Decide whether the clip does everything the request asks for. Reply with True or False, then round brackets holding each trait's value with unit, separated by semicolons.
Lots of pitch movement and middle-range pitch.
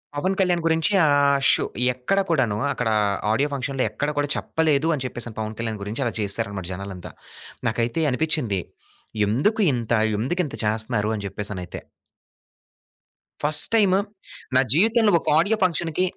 False (7.2 semitones; 130 Hz)